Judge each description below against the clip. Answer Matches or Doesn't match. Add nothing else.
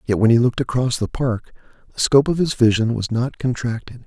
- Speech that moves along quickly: Matches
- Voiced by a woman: Doesn't match